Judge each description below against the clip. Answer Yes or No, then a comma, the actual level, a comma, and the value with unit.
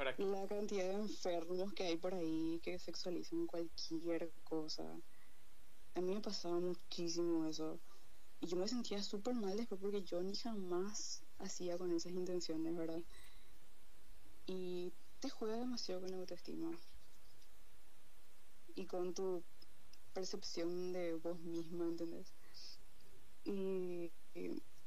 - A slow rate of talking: Yes, slow, 120 wpm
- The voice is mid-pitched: Yes, medium, 180 Hz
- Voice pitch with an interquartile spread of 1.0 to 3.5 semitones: Yes, narrow, 2.5 semitones